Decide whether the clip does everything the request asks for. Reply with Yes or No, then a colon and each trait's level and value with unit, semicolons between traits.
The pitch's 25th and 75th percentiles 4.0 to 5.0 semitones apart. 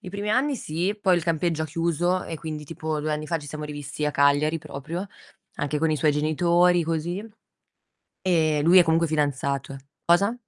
No: narrow, 2.6 semitones